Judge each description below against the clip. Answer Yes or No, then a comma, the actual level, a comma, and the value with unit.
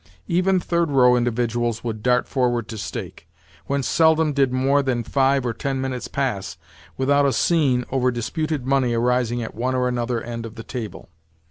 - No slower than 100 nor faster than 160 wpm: No, average, 175 wpm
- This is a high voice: No, low, 125 Hz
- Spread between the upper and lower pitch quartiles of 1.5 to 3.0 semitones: Yes, narrow, 2.6 semitones